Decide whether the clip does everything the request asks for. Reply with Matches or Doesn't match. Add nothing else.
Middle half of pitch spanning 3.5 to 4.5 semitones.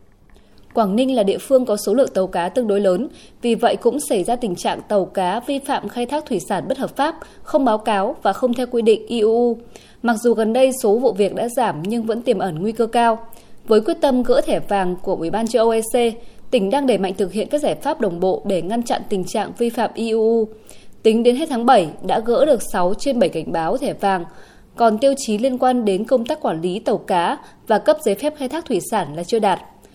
Matches